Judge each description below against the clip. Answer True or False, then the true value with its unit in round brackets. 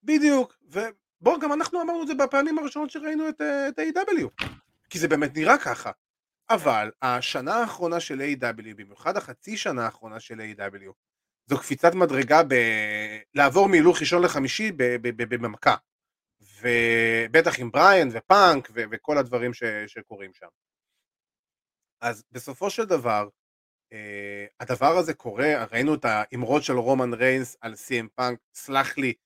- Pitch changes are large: True (8.1 semitones)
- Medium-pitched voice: False (130 Hz)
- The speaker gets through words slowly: False (140 wpm)